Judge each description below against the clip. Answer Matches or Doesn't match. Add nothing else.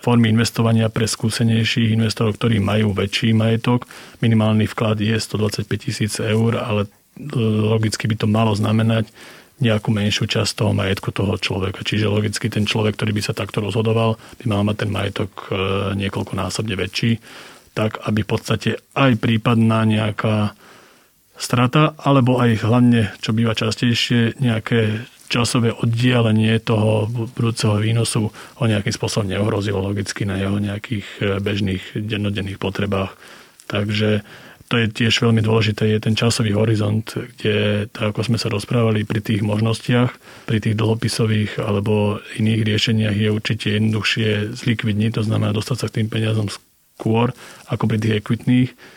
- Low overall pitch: Matches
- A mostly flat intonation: Matches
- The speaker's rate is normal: Matches